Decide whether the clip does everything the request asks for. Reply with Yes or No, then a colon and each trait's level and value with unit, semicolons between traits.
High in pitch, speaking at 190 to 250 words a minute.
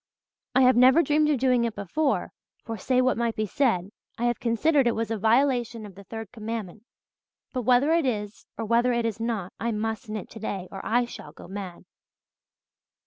Yes: high, 230 Hz; average, 195 wpm